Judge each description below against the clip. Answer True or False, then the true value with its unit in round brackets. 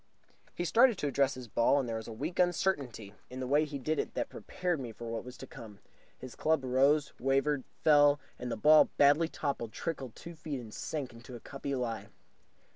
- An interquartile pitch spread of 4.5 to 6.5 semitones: False (4.0 semitones)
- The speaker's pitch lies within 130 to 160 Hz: True (140 Hz)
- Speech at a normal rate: False (210 wpm)